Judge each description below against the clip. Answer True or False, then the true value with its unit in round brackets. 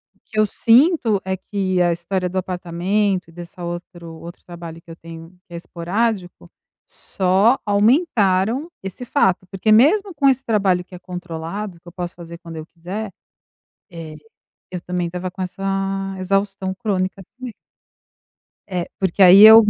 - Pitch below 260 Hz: True (185 Hz)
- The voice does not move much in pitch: False (3.3 semitones)